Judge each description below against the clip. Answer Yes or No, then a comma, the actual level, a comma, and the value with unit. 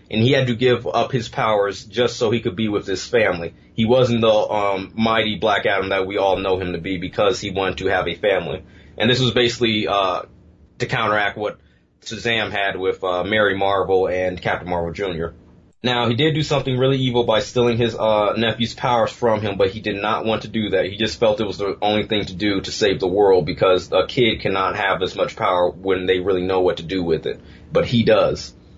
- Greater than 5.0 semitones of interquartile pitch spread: No, average, 3.8 semitones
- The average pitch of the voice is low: Yes, low, 105 Hz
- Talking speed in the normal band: No, fast, 235 wpm